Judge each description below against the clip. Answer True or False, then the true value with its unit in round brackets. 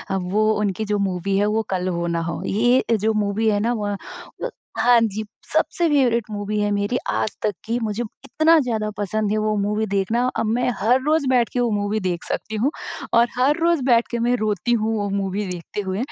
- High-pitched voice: True (215 Hz)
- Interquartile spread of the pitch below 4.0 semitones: True (2.9 semitones)